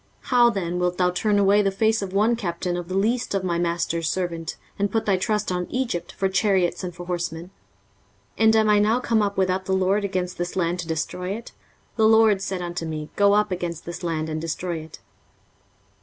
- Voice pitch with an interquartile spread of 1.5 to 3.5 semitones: Yes, average, 3.0 semitones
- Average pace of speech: No, fast, 220 wpm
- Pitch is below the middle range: No, medium, 185 Hz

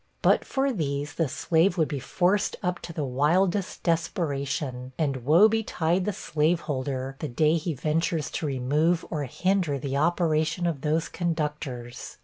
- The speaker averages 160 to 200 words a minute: No, average, 150 wpm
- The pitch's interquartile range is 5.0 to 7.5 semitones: No, average, 3.7 semitones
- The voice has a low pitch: No, medium, 155 Hz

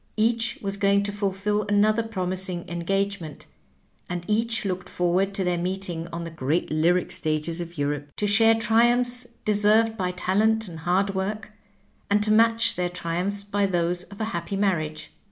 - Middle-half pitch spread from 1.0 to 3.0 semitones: No, average, 3.4 semitones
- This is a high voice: Yes, high, 195 Hz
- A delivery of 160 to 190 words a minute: Yes, average, 170 wpm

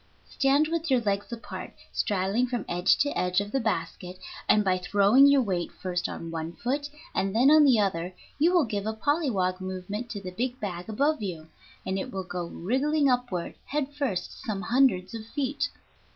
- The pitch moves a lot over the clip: Yes, wide, 6.6 semitones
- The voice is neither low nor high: No, high, 210 Hz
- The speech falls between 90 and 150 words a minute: No, average, 190 wpm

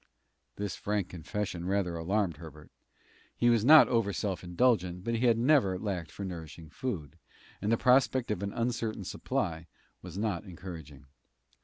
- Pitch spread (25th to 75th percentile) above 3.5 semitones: Yes, average, 4.8 semitones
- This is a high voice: No, low, 100 Hz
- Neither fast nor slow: Yes, average, 155 wpm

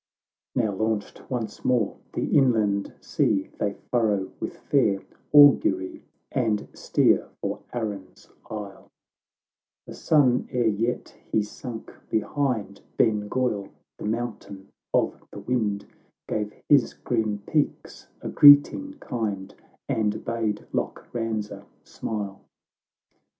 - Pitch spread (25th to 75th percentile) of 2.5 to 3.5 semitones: Yes, average, 3.2 semitones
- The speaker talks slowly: Yes, slow, 115 wpm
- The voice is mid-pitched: No, low, 110 Hz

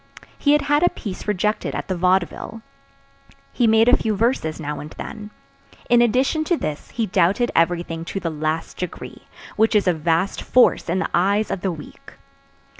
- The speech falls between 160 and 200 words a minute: Yes, average, 185 wpm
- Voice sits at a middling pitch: No, high, 195 Hz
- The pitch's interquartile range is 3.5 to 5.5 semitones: Yes, average, 5.2 semitones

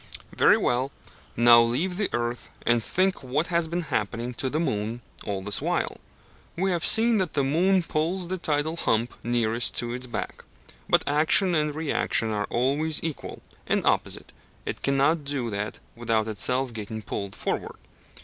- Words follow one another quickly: No, average, 165 wpm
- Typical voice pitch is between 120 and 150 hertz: Yes, low, 135 Hz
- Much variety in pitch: Yes, wide, 5.7 semitones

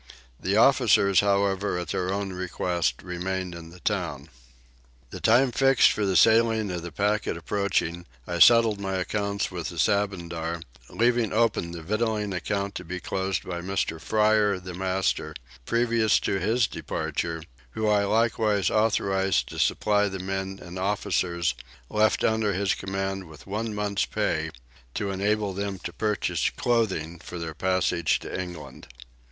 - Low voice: Yes, very low, 95 Hz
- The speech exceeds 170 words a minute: No, average, 150 wpm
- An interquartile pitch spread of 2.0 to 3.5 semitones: Yes, average, 3.1 semitones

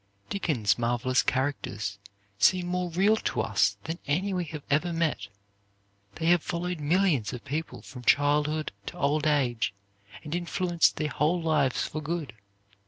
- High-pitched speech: No, medium, 155 Hz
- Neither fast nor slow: Yes, average, 150 wpm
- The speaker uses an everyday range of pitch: Yes, average, 4.1 semitones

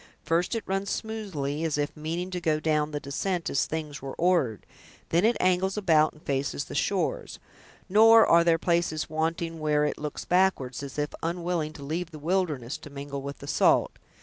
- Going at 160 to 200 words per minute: Yes, average, 190 wpm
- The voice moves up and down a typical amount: Yes, average, 3.4 semitones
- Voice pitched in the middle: Yes, medium, 160 Hz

